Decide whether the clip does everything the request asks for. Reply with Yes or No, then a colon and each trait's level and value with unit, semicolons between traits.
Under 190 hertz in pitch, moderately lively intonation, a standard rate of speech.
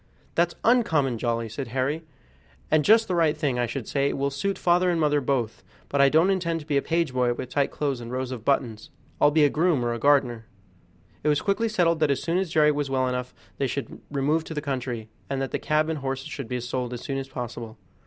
No: medium, 140 Hz; average, 3.9 semitones; fast, 245 wpm